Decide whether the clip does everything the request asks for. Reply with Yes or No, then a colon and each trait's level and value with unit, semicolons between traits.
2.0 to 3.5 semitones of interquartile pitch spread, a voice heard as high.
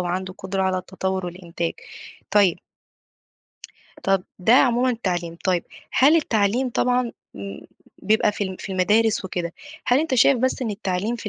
No: average, 4.5 semitones; high, 195 Hz